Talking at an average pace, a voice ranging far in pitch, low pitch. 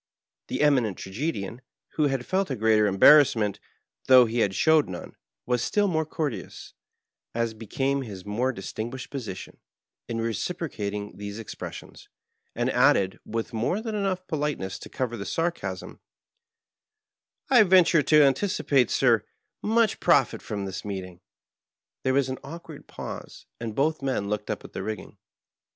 Yes: average, 145 wpm; wide, 6.5 semitones; low, 125 Hz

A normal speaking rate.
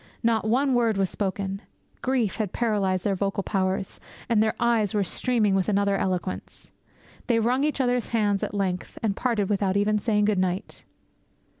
Yes: average, 170 wpm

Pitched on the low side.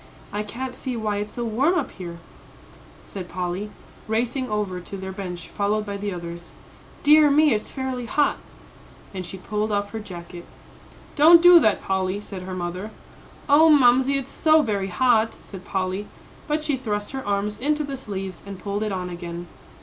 No: high, 210 Hz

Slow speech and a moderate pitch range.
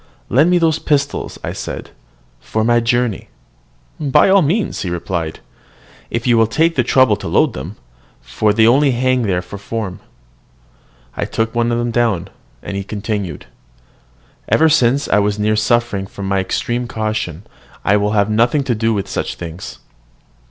No: average, 170 wpm; average, 3.8 semitones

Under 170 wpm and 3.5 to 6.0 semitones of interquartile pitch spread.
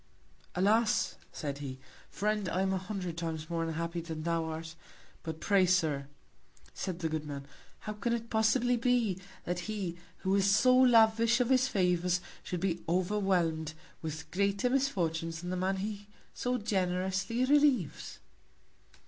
Yes: average, 150 wpm; average, 4.7 semitones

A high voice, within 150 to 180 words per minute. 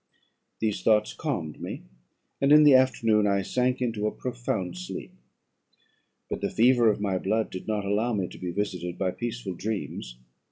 No: low, 105 Hz; average, 170 wpm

